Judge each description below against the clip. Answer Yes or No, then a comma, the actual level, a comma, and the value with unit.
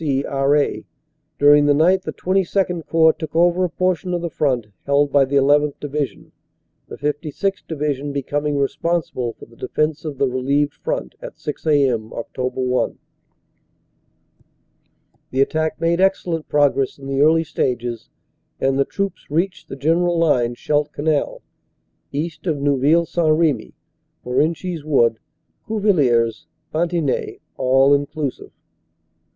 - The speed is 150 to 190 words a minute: No, average, 140 wpm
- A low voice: No, medium, 145 Hz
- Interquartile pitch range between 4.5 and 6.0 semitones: No, average, 3.3 semitones